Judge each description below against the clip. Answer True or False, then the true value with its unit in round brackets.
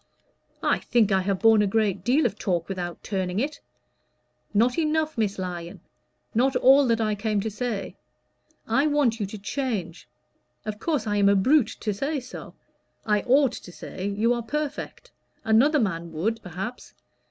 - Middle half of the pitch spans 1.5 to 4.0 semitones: False (4.7 semitones)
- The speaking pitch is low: False (220 Hz)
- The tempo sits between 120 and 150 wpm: False (170 wpm)